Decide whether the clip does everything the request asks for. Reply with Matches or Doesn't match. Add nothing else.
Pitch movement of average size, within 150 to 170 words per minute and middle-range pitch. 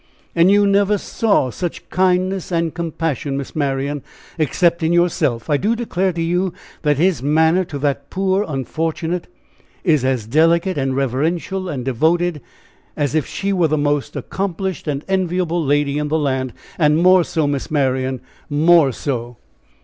Matches